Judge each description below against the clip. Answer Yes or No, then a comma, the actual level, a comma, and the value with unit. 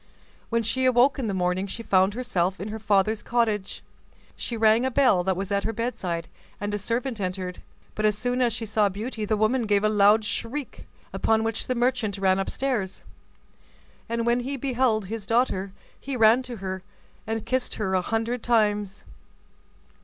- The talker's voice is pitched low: No, high, 220 Hz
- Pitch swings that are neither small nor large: Yes, average, 3.4 semitones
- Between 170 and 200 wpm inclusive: Yes, average, 185 wpm